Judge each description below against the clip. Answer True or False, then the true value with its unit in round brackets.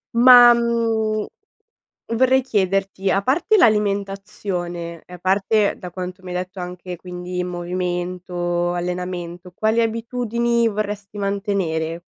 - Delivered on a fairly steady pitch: False (3.7 semitones)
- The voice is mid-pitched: False (195 Hz)